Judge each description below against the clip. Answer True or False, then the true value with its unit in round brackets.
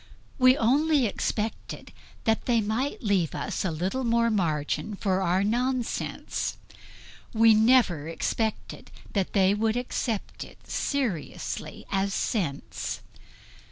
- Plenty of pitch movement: False (4.1 semitones)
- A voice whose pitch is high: True (220 Hz)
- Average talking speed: False (115 wpm)